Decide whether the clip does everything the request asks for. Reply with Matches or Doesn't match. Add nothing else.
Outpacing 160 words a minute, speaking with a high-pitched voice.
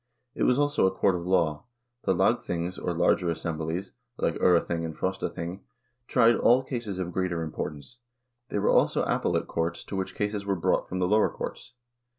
Doesn't match